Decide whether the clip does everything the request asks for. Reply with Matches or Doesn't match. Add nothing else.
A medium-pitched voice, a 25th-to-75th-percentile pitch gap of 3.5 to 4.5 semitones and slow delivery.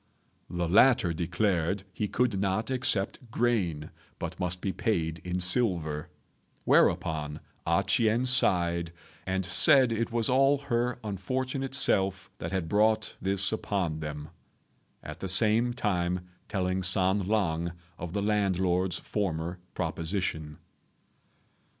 Doesn't match